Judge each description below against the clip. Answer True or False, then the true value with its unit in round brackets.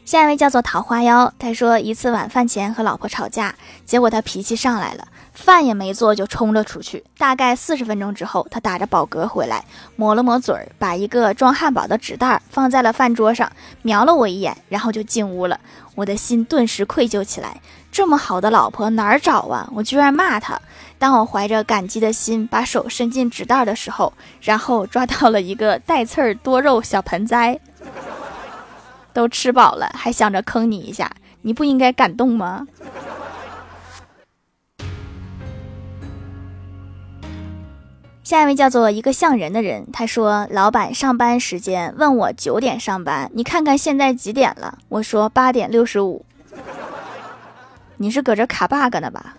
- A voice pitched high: True (230 Hz)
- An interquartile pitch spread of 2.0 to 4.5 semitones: True (3.8 semitones)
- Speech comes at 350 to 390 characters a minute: False (250 characters per minute)